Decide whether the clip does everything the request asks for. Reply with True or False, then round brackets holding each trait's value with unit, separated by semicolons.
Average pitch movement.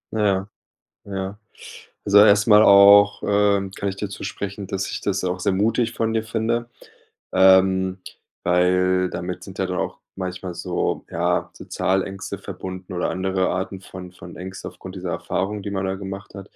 False (1.6 semitones)